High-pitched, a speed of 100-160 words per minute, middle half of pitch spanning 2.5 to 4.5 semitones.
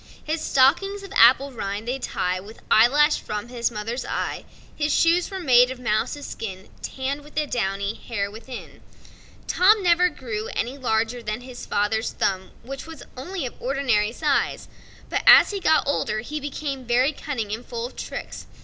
No: very high, 250 Hz; average, 155 wpm; average, 5.1 semitones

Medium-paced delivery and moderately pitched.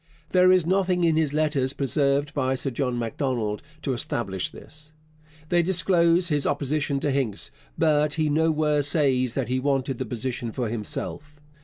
Yes: average, 160 wpm; medium, 145 Hz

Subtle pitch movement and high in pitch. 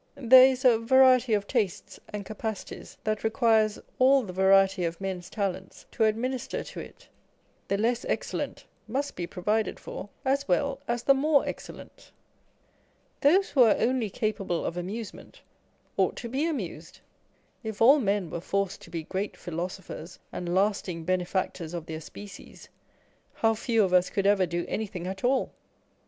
No: average, 4.9 semitones; high, 210 Hz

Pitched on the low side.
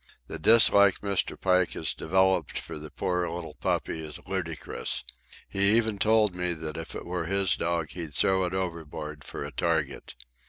Yes: very low, 90 Hz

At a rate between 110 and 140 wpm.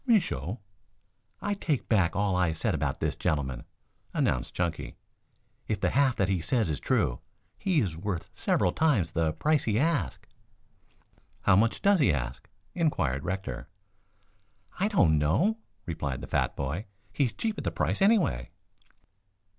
No: average, 155 wpm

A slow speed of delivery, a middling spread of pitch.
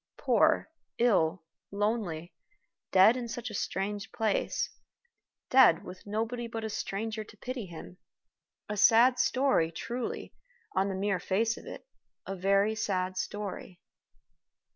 Yes: slow, 125 wpm; average, 3.5 semitones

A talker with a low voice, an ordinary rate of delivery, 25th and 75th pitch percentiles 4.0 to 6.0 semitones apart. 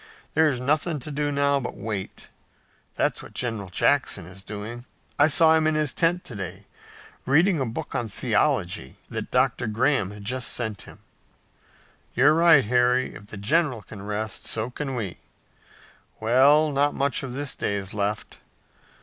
Yes: low, 125 Hz; average, 165 wpm; wide, 5.6 semitones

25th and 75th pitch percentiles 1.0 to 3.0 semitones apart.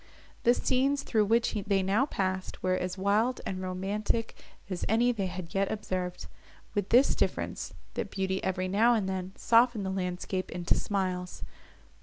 No: average, 3.4 semitones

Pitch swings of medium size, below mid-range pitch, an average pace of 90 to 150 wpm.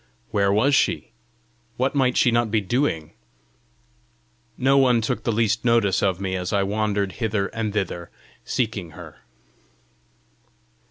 Yes: average, 3.2 semitones; low, 110 Hz; average, 140 wpm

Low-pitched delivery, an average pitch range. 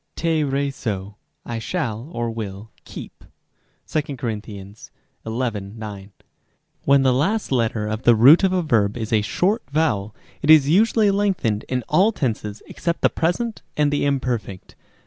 No: low, 125 Hz; wide, 6.5 semitones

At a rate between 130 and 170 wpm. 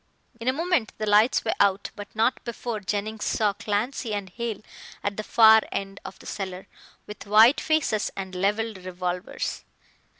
Yes: average, 165 wpm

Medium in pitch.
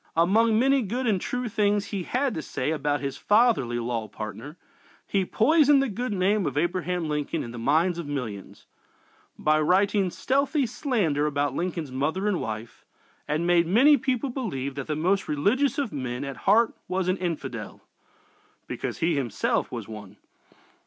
Yes: medium, 175 Hz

